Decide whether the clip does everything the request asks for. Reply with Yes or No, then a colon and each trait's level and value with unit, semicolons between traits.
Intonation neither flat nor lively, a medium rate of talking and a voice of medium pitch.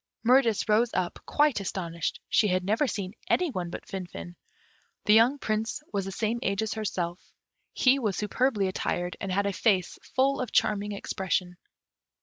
No: average, 3.9 semitones; average, 165 wpm; high, 205 Hz